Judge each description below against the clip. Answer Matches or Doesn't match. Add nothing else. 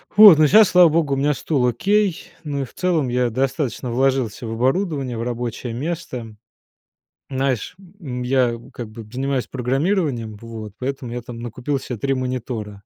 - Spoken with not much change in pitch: Doesn't match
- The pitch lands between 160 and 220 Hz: Doesn't match